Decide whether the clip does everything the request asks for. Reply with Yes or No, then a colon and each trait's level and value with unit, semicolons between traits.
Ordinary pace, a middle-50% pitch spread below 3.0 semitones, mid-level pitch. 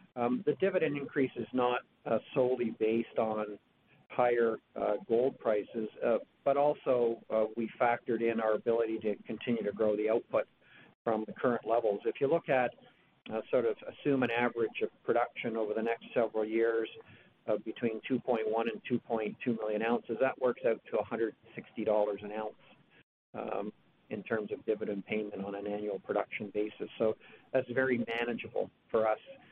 No: average, 165 wpm; narrow, 2.4 semitones; low, 115 Hz